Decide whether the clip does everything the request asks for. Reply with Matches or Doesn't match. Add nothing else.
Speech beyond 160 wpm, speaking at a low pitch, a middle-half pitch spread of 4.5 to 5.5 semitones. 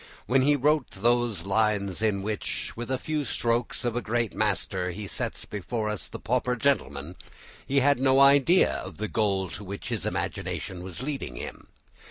Matches